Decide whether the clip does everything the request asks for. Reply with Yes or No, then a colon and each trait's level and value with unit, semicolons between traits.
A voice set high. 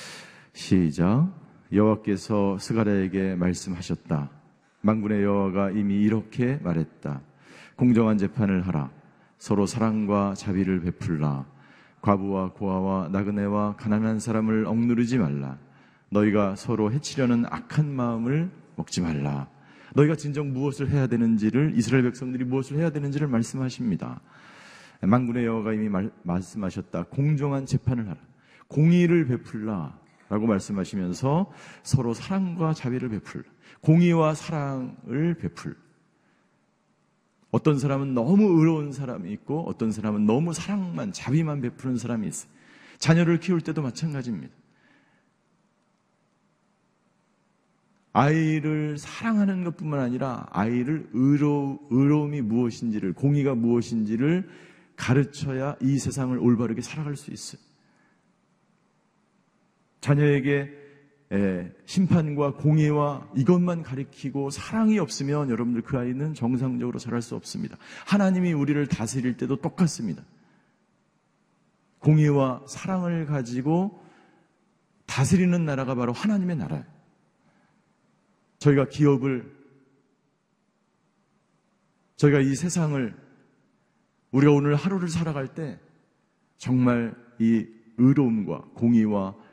No: low, 135 Hz